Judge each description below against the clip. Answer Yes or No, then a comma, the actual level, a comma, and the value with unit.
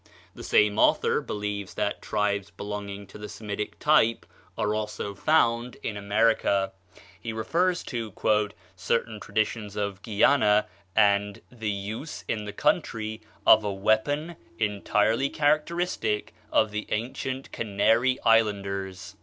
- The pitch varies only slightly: Yes, narrow, 2.2 semitones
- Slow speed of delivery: Yes, slow, 120 wpm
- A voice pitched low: Yes, low, 105 Hz